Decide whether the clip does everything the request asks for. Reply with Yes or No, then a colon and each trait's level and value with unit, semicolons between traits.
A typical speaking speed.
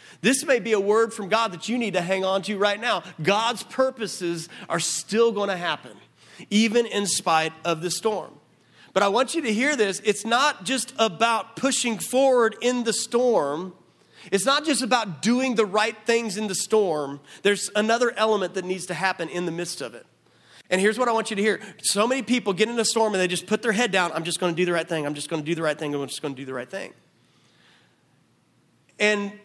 No: fast, 235 wpm